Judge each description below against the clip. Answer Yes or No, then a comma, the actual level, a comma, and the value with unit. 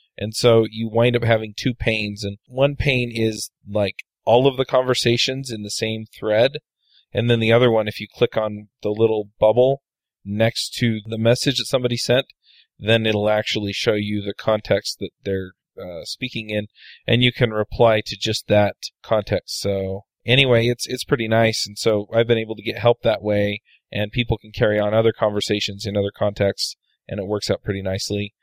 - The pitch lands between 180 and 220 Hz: No, low, 110 Hz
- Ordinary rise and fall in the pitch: No, narrow, 2.3 semitones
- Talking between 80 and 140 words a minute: No, average, 195 wpm